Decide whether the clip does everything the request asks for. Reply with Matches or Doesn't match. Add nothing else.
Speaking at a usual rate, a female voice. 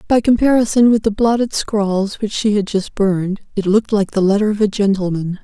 Doesn't match